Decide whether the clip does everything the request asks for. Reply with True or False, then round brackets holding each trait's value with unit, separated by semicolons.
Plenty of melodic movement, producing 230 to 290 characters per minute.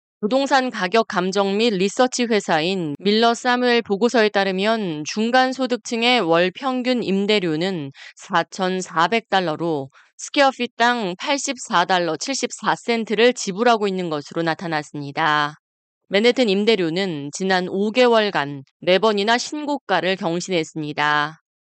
True (6.1 semitones; 255 characters per minute)